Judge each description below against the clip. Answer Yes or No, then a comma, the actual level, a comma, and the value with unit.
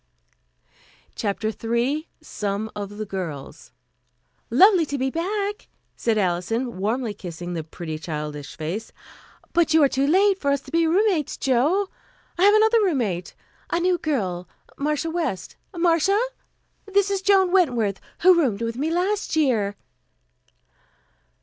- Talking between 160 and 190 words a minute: No, slow, 135 wpm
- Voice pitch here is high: Yes, very high, 275 Hz